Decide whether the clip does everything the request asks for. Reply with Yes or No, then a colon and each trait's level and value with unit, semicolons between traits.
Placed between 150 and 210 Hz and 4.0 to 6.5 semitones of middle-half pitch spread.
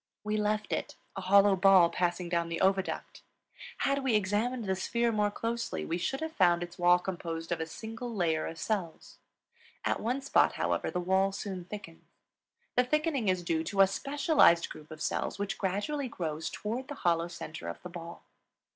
Yes: high, 190 Hz; average, 4.6 semitones